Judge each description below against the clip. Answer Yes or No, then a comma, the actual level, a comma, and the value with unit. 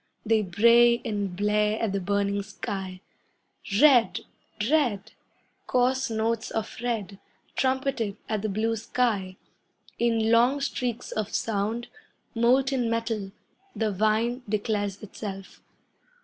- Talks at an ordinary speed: No, slow, 110 wpm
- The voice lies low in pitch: No, high, 220 Hz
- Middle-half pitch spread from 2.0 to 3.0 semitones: Yes, average, 2.7 semitones